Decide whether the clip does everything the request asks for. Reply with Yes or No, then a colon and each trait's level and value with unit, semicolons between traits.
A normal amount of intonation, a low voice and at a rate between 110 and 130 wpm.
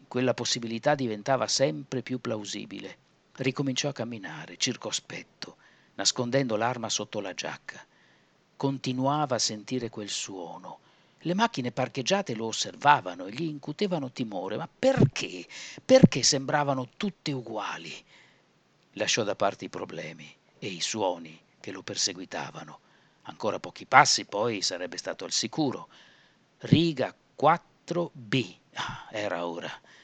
Yes: average, 4.5 semitones; low, 130 Hz; average, 120 wpm